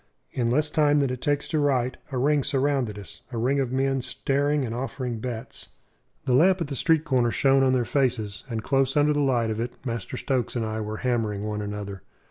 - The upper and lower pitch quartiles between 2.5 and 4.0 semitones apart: Yes, average, 3.6 semitones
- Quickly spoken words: Yes, fast, 220 wpm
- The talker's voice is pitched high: No, low, 130 Hz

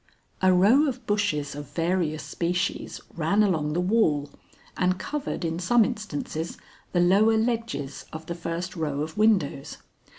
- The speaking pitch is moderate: Yes, medium, 180 Hz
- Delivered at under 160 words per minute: Yes, average, 145 wpm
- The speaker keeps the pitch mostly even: No, average, 5.1 semitones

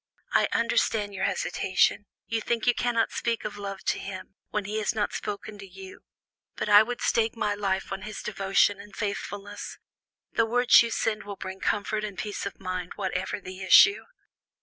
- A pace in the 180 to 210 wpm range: Yes, average, 190 wpm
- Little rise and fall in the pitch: Yes, narrow, 2.0 semitones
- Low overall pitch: No, high, 205 Hz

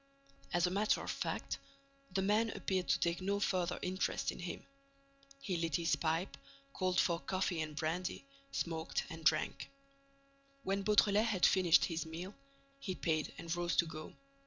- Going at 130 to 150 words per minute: No, average, 160 wpm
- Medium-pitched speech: Yes, medium, 180 Hz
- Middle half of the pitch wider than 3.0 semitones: No, average, 2.7 semitones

